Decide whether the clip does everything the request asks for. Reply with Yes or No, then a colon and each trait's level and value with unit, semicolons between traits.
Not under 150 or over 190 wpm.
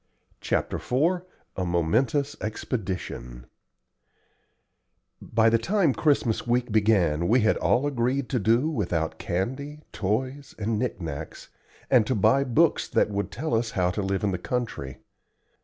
No: average, 140 wpm